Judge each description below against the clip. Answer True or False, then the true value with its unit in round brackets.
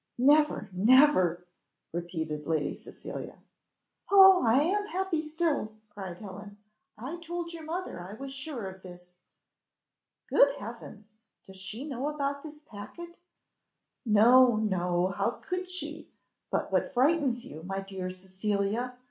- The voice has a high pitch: True (235 Hz)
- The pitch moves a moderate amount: False (8.0 semitones)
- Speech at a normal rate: False (130 wpm)